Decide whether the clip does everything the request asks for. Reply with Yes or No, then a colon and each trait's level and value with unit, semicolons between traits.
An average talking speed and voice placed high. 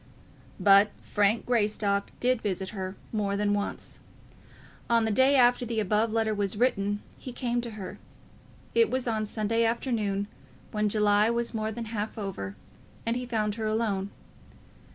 Yes: average, 155 wpm; high, 215 Hz